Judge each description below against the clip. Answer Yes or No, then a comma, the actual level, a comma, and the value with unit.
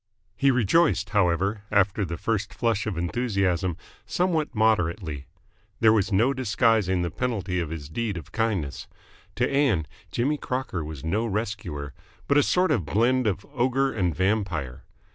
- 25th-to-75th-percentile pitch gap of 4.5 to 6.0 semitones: Yes, wide, 5.4 semitones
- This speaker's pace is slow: No, average, 150 wpm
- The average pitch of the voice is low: Yes, low, 105 Hz